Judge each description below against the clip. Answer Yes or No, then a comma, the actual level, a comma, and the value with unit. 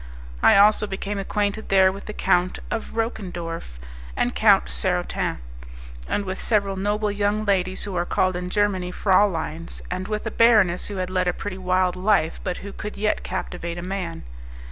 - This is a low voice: No, high, 190 Hz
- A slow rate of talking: No, average, 175 wpm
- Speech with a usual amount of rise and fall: No, narrow, 2.3 semitones